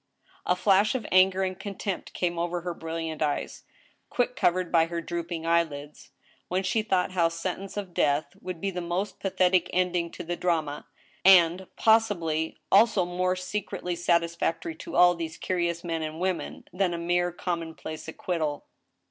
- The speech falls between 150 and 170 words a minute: Yes, average, 165 wpm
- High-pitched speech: No, medium, 175 Hz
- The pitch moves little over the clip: Yes, narrow, 1.9 semitones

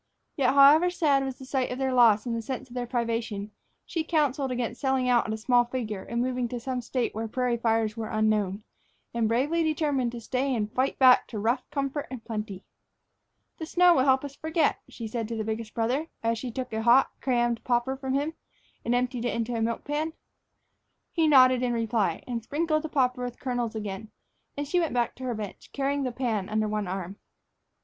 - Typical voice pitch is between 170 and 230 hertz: No, high, 245 Hz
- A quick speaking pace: Yes, fast, 215 wpm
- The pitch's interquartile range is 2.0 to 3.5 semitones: Yes, average, 3.0 semitones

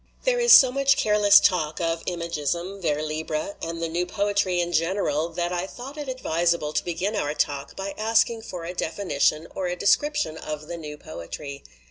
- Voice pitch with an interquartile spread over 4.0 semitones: Yes, average, 4.4 semitones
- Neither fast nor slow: Yes, average, 185 wpm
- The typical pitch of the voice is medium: Yes, medium, 175 Hz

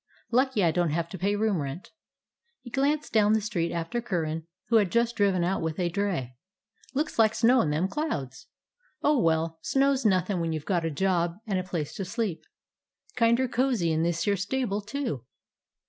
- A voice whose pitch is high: Yes, high, 195 Hz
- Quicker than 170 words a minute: Yes, average, 195 wpm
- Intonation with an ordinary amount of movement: No, wide, 5.8 semitones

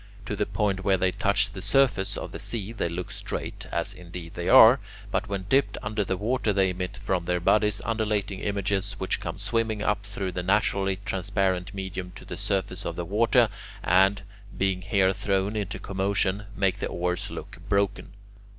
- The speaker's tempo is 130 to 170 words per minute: No, average, 185 wpm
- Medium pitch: No, low, 100 Hz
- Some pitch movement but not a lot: No, narrow, 1.8 semitones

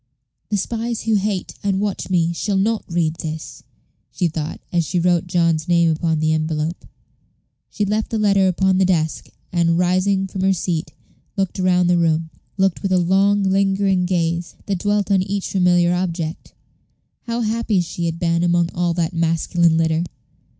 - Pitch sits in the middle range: Yes, medium, 180 Hz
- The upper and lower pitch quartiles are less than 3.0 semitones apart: Yes, narrow, 2.6 semitones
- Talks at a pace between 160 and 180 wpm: Yes, average, 170 wpm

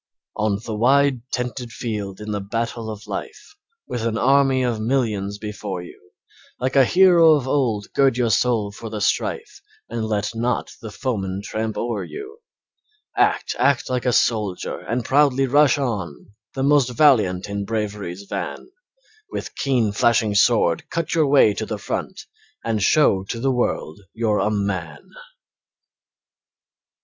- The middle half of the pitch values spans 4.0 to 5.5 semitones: Yes, average, 4.3 semitones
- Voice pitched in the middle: No, low, 115 Hz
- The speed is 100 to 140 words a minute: No, average, 155 wpm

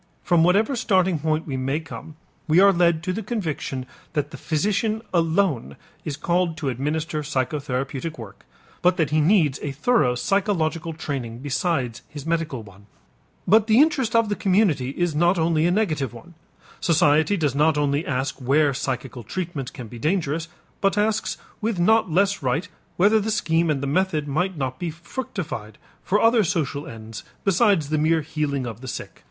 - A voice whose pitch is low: No, medium, 160 Hz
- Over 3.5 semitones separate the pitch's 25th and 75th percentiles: Yes, average, 5.1 semitones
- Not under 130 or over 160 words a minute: No, average, 175 wpm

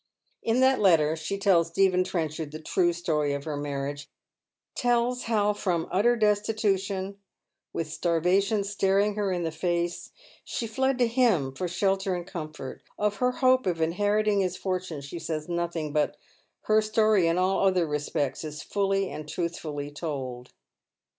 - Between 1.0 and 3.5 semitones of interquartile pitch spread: No, average, 4.5 semitones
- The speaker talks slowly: No, average, 160 wpm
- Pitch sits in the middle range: Yes, medium, 180 Hz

